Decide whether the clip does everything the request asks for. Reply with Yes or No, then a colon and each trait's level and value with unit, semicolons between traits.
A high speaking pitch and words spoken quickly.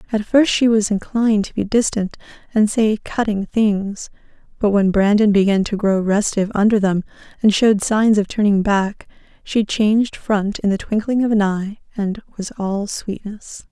No: high, 210 Hz; average, 175 wpm